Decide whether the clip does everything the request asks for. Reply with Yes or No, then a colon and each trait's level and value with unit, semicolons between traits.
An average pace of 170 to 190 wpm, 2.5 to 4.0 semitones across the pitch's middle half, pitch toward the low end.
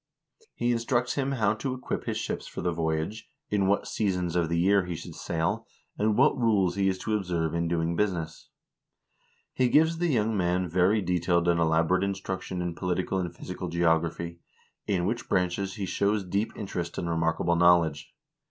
Yes: average, 180 wpm; average, 3.4 semitones; very low, 90 Hz